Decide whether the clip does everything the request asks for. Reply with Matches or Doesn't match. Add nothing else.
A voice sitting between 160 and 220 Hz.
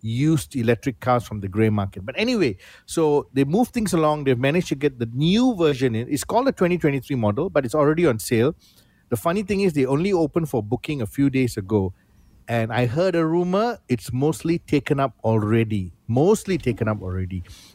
Doesn't match